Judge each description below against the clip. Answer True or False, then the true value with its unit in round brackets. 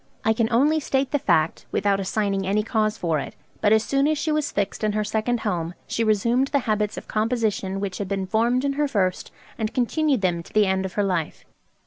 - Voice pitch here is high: True (215 Hz)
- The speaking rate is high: True (230 wpm)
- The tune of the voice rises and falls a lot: False (4.2 semitones)